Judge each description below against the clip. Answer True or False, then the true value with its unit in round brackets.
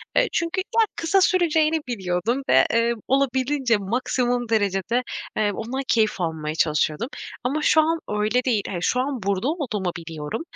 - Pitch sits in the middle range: False (235 Hz)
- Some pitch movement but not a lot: False (5.8 semitones)